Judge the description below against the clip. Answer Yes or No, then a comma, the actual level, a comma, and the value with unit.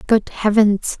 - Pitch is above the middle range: Yes, high, 210 Hz